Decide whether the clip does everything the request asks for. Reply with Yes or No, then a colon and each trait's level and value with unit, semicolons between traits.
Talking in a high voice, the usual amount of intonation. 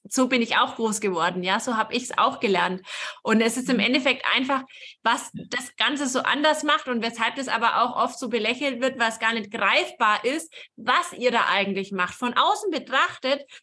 Yes: high, 245 Hz; average, 3.2 semitones